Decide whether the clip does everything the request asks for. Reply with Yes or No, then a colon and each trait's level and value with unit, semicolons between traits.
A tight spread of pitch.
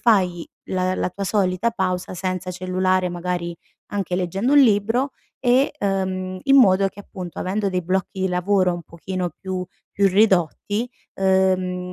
Yes: narrow, 1.7 semitones